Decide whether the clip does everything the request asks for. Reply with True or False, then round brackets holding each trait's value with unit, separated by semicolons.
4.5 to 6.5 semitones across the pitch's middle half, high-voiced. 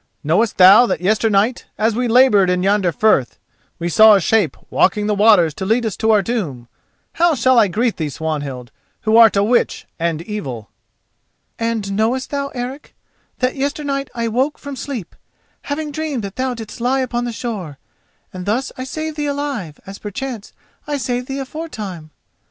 True (5.1 semitones; 225 Hz)